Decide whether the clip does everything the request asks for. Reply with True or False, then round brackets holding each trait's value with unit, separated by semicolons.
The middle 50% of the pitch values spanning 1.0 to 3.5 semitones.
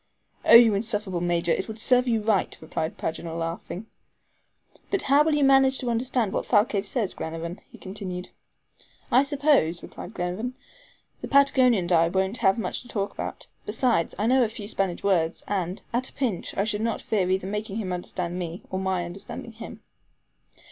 False (5.0 semitones)